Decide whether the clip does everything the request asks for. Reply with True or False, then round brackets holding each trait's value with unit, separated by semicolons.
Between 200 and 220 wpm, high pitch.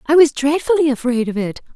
True (205 wpm; 280 Hz)